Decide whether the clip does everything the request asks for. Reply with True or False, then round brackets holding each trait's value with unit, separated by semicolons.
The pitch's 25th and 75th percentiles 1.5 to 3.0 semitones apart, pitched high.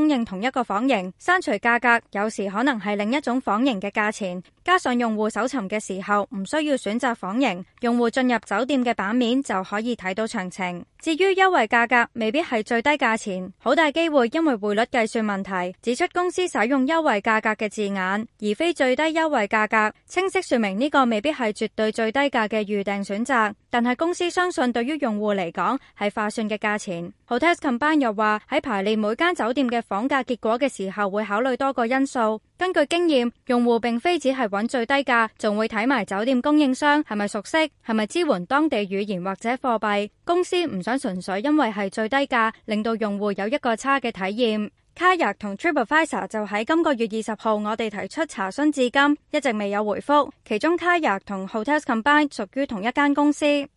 False (5.1 semitones; 235 Hz)